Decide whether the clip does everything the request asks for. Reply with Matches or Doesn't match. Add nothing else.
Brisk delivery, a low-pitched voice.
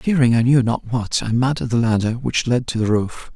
Matches